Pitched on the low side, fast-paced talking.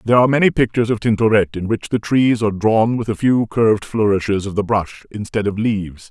Yes: low, 110 Hz; fast, 225 wpm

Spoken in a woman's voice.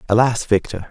No: male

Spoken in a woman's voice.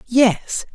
Yes: female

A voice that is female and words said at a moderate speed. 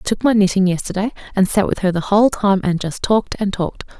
No: female; fast, 255 wpm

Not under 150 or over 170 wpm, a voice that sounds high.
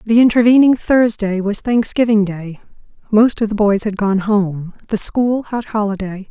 Yes: average, 160 wpm; high, 215 Hz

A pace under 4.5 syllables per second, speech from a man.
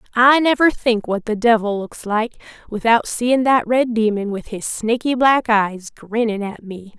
No: 4.3 syllables/s; female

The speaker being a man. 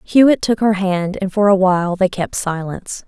No: female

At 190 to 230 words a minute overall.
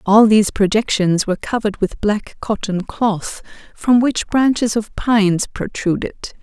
No: average, 140 wpm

